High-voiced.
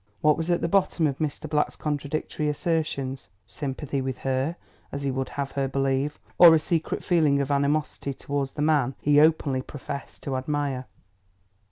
No: medium, 145 Hz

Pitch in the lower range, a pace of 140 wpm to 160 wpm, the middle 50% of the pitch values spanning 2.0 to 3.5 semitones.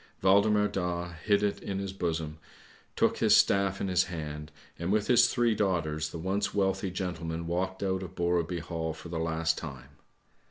No: very low, 90 Hz; average, 175 wpm; average, 3.1 semitones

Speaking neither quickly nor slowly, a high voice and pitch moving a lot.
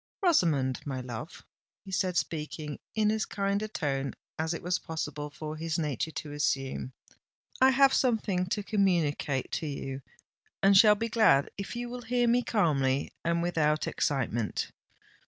No: average, 155 wpm; medium, 165 Hz; wide, 6.4 semitones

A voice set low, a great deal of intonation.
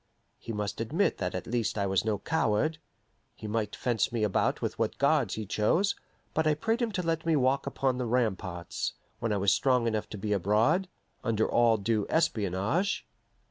Yes: low, 115 Hz; wide, 6.5 semitones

